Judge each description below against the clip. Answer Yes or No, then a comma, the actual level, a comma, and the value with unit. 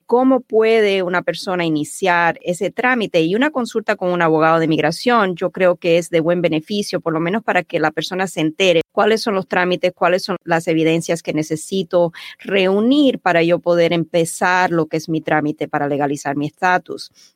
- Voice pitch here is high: No, medium, 175 Hz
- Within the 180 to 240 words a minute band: Yes, fast, 190 wpm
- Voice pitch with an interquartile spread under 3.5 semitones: Yes, average, 2.9 semitones